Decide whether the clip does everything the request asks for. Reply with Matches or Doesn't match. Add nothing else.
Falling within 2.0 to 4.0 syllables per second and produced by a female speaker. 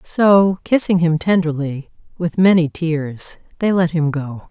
Matches